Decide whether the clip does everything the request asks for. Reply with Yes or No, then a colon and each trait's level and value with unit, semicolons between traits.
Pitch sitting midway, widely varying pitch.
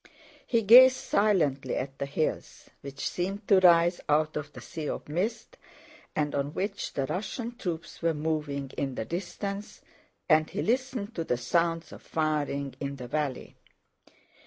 Yes: medium, 160 Hz; wide, 5.8 semitones